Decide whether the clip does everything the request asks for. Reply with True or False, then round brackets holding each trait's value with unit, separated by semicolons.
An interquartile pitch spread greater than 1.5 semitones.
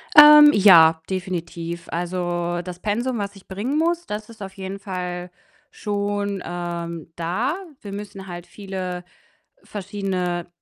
True (2.8 semitones)